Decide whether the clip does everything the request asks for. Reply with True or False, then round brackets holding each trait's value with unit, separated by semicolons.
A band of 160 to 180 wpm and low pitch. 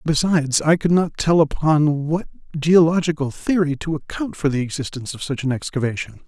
False (170 wpm; 155 Hz)